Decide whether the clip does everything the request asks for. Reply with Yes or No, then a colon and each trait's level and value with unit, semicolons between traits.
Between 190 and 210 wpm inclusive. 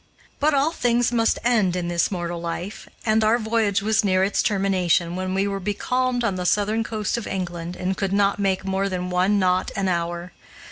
Yes: average, 200 wpm